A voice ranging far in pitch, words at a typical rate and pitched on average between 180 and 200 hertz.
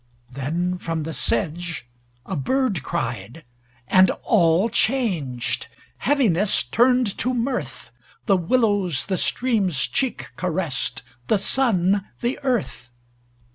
No: wide, 6.6 semitones; slow, 105 wpm; medium, 185 Hz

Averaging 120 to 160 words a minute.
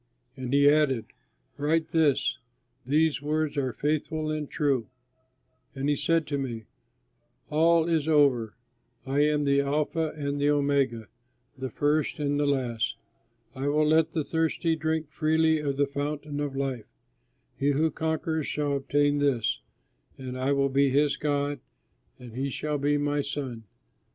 Yes: average, 150 wpm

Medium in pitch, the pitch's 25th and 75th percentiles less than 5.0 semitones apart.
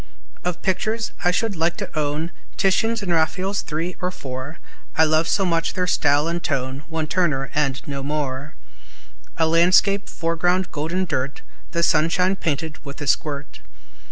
Yes: medium, 165 Hz; average, 3.6 semitones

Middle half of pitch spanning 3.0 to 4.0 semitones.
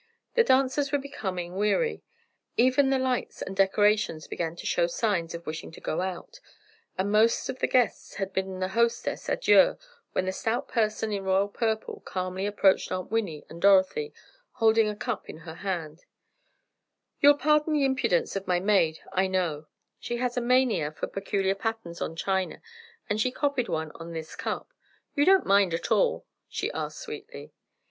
No: wide, 5.6 semitones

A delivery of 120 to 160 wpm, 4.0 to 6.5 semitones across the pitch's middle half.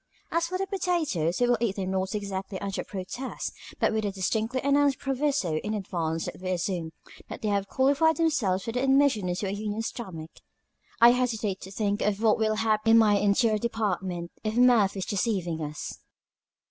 No: average, 185 wpm; average, 4.6 semitones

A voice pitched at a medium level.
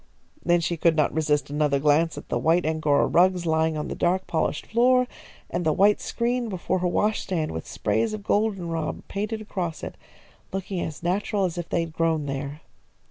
Yes: medium, 170 Hz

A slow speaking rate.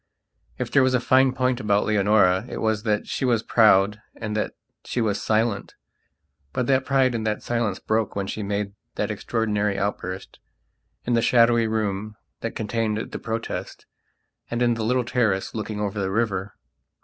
No: average, 175 wpm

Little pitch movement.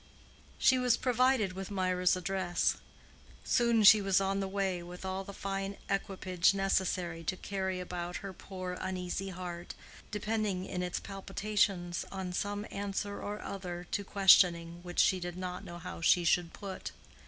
Yes: narrow, 1.8 semitones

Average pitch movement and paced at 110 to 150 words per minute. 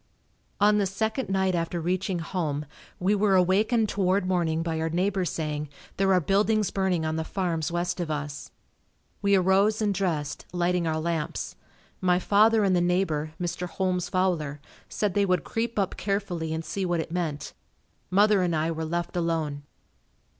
No: average, 3.2 semitones; average, 170 wpm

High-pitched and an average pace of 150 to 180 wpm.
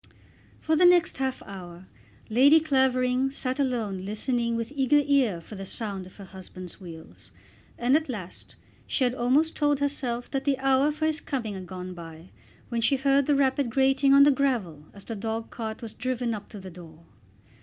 No: high, 245 Hz; average, 190 wpm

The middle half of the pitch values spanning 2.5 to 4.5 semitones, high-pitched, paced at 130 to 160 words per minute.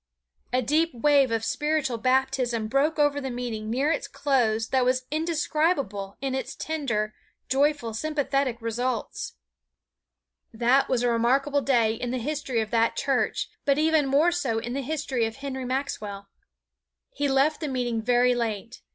Yes: average, 3.7 semitones; very high, 260 Hz; average, 155 wpm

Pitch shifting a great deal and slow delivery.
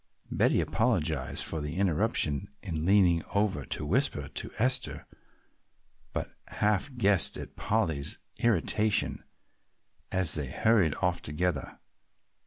Yes: wide, 5.8 semitones; slow, 110 wpm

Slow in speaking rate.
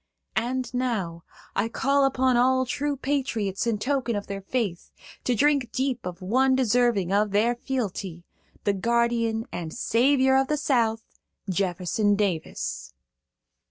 Yes: slow, 125 wpm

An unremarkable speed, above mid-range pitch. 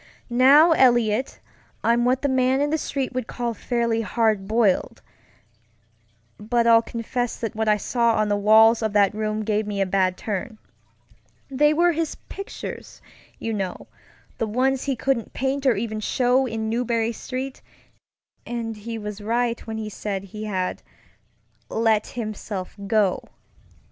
Yes: average, 150 wpm; high, 225 Hz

